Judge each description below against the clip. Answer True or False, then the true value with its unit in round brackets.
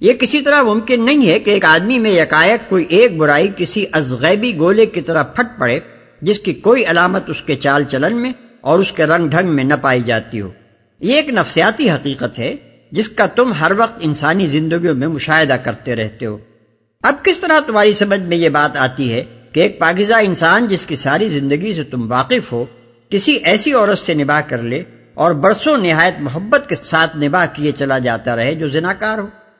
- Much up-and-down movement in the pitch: True (7.2 semitones)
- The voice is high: False (165 Hz)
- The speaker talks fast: True (205 wpm)